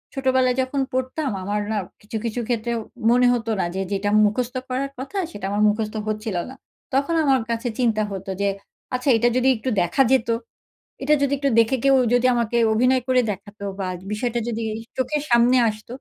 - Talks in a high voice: Yes, high, 240 Hz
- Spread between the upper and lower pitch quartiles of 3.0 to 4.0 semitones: Yes, average, 3.3 semitones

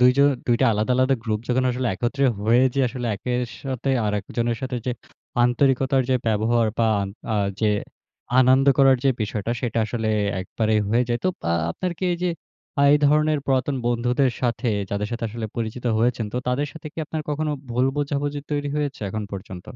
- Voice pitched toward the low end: Yes, low, 125 Hz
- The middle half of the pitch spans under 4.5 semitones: Yes, average, 3.3 semitones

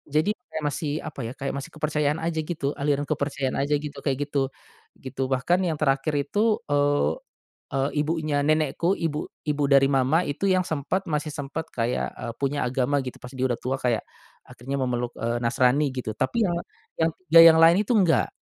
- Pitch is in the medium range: Yes, medium, 145 Hz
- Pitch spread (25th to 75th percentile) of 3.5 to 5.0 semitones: No, average, 3.0 semitones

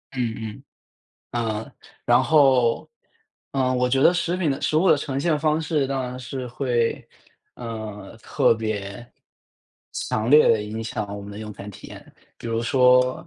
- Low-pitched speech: Yes, low, 125 Hz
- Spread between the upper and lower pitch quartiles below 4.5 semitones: Yes, average, 3.7 semitones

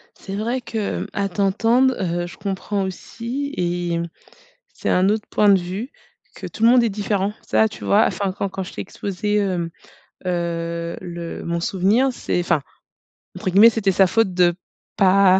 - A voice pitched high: Yes, high, 195 Hz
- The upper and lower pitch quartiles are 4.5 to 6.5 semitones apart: No, average, 3.4 semitones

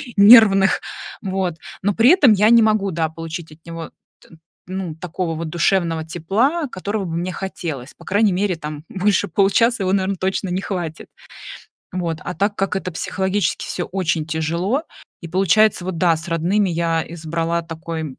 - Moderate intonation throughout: Yes, average, 3.3 semitones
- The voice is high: No, medium, 180 Hz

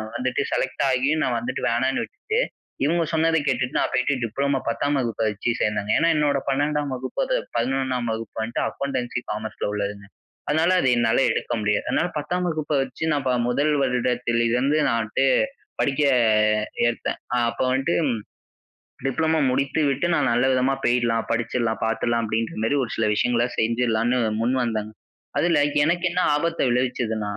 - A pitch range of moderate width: Yes, average, 3.7 semitones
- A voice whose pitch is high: No, low, 125 Hz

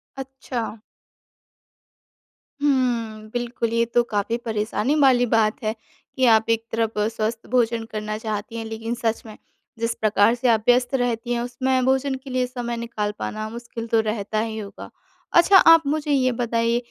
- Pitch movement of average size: No, narrow, 2.2 semitones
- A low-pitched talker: No, high, 230 Hz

